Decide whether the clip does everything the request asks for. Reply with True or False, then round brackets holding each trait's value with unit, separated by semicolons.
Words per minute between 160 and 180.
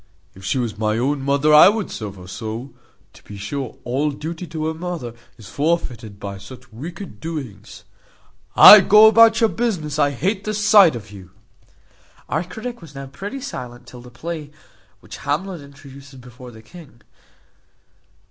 True (165 wpm)